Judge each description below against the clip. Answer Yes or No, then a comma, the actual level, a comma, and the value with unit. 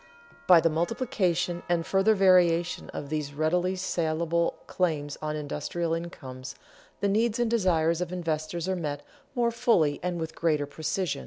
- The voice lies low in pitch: No, medium, 170 Hz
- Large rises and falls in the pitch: No, average, 2.9 semitones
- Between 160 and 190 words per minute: No, average, 150 wpm